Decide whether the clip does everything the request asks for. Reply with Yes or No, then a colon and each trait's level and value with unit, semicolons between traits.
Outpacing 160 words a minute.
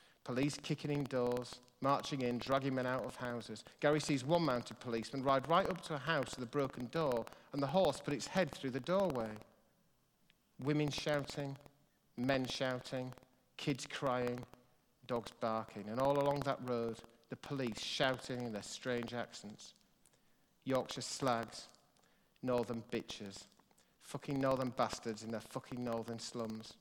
No: average, 150 wpm